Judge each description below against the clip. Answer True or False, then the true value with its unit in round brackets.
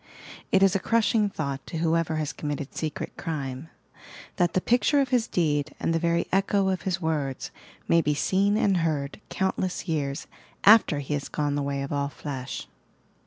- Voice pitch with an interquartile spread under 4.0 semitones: False (4.8 semitones)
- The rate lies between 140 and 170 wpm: False (185 wpm)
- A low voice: False (160 Hz)